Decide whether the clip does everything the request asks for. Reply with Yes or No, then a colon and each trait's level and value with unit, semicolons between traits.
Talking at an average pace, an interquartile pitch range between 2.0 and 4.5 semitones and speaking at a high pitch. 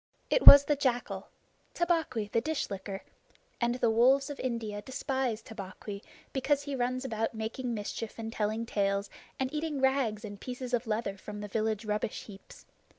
Yes: average, 165 wpm; average, 3.9 semitones; high, 230 Hz